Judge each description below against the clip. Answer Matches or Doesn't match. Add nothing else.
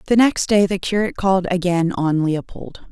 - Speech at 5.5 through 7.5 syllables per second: Doesn't match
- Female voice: Matches